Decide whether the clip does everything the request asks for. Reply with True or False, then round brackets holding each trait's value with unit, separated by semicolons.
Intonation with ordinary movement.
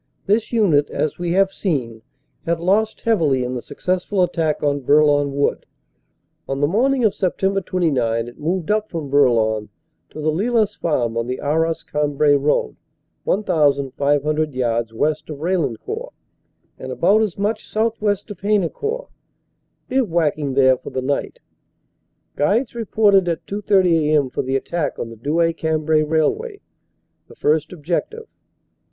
False (5.8 semitones)